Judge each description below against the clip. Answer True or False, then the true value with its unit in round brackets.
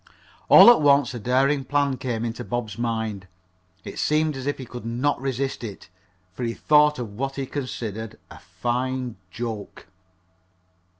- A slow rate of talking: False (160 wpm)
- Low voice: True (125 Hz)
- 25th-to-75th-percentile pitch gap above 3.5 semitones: False (3.2 semitones)